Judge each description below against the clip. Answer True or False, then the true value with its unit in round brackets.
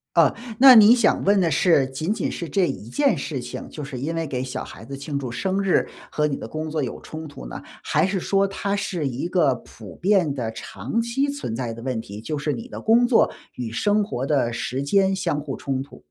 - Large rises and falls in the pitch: True (7.2 semitones)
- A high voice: False (150 Hz)